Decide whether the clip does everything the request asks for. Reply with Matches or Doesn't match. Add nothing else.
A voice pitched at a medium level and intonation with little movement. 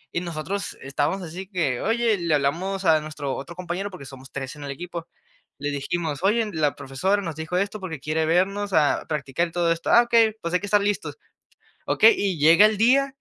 Doesn't match